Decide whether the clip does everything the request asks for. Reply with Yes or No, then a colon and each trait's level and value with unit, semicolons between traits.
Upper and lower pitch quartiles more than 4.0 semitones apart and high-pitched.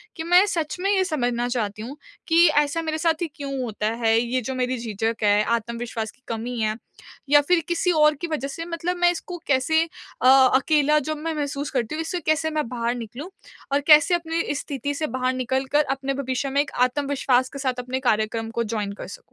Yes: average, 4.6 semitones; very high, 275 Hz